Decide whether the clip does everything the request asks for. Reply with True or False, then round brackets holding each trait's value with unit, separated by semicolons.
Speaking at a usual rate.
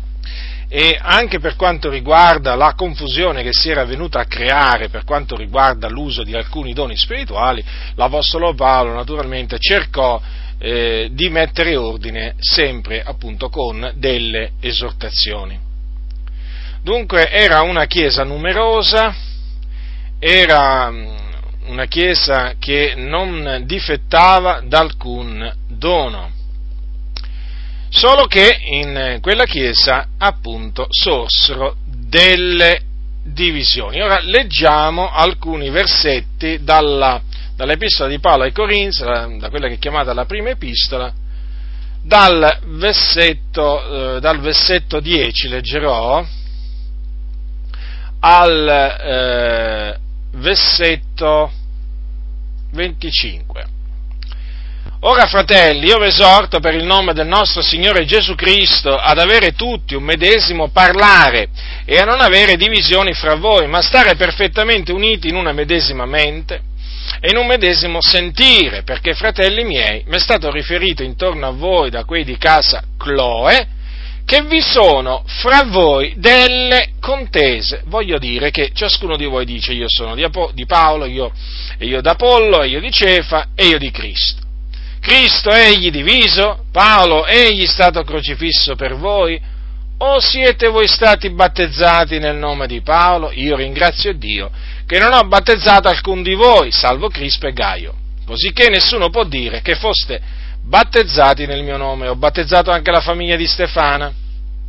True (125 wpm)